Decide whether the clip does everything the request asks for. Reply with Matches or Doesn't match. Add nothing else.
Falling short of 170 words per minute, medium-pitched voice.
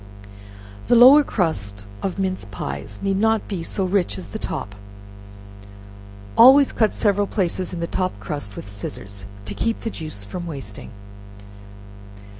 Matches